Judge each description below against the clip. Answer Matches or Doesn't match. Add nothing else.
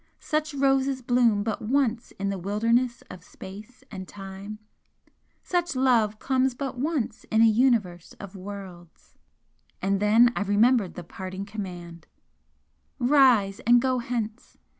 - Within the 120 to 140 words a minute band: Matches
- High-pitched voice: Matches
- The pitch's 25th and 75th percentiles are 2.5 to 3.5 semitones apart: Doesn't match